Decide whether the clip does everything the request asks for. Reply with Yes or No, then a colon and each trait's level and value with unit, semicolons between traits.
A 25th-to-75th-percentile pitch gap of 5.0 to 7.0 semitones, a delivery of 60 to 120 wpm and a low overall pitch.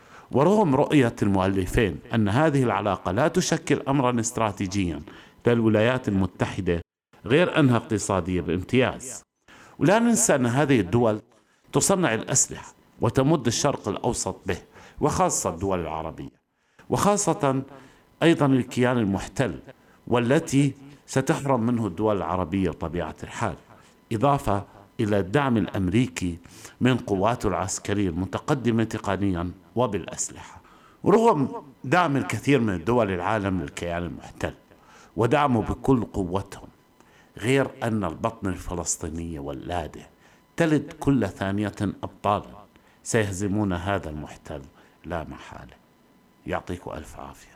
Yes: wide, 5.6 semitones; average, 100 wpm; low, 110 Hz